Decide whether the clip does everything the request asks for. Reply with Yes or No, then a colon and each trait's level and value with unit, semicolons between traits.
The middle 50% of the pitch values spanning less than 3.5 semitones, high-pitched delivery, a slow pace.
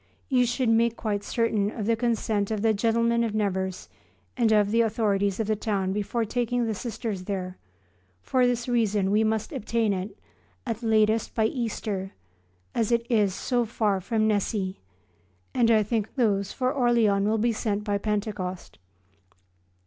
No: narrow, 2.4 semitones; high, 220 Hz; average, 165 wpm